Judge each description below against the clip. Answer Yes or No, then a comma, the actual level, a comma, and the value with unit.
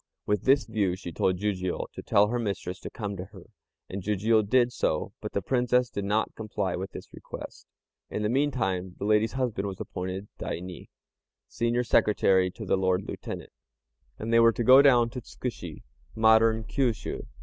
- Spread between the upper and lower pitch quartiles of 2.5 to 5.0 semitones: Yes, average, 3.8 semitones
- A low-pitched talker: Yes, low, 105 Hz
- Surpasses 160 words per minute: Yes, average, 180 wpm